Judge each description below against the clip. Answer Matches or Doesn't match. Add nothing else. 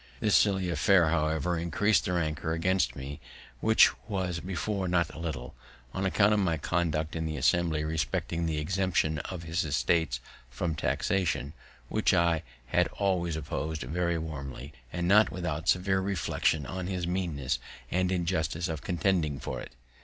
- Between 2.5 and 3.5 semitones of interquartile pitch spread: Matches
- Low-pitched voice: Matches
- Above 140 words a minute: Matches